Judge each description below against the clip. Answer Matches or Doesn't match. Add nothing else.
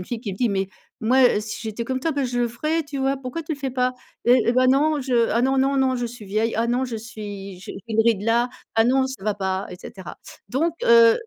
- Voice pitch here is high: Matches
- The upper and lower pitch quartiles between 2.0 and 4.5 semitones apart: Matches